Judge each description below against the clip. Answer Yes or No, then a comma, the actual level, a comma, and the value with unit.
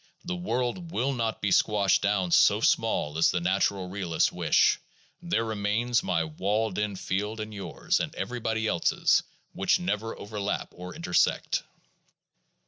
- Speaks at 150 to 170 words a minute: No, average, 140 wpm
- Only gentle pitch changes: No, average, 3.3 semitones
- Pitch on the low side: Yes, low, 105 Hz